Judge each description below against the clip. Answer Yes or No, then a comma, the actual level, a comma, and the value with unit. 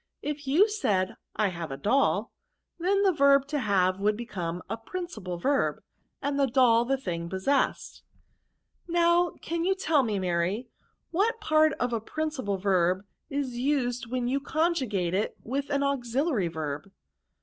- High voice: Yes, very high, 255 Hz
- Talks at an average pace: Yes, average, 160 wpm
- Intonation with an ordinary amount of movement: No, wide, 7.3 semitones